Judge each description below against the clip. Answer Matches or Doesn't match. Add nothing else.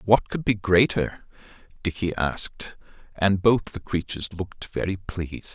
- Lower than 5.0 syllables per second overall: Matches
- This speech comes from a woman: Doesn't match